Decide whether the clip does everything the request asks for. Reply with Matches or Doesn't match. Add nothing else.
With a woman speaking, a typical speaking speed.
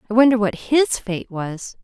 Matches